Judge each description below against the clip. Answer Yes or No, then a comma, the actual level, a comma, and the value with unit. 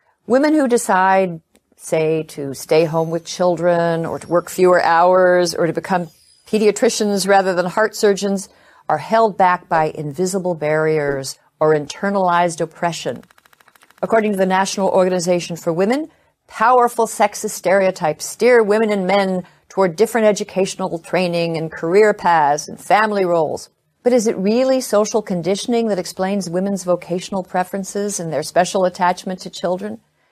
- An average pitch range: Yes, average, 3.5 semitones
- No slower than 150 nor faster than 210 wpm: No, average, 140 wpm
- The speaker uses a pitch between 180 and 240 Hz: Yes, medium, 185 Hz